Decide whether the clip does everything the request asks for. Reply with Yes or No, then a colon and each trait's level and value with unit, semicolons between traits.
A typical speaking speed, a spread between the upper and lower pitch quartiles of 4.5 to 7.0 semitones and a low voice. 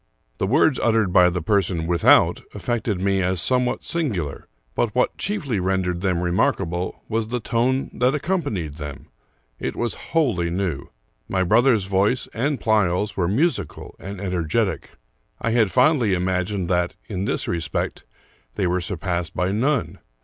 Yes: average, 155 wpm; average, 5.1 semitones; very low, 95 Hz